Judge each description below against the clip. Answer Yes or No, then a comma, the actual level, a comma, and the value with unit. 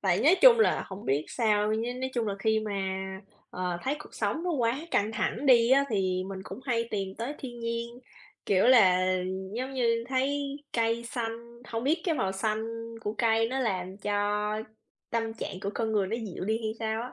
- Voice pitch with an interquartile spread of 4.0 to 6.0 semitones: No, average, 3.2 semitones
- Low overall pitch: No, high, 230 Hz